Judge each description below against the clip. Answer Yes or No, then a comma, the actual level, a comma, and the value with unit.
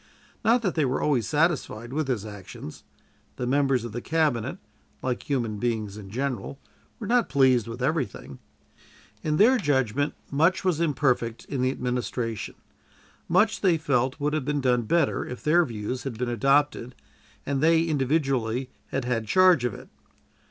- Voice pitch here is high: No, low, 135 Hz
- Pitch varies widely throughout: No, average, 4.3 semitones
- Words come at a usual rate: Yes, average, 160 wpm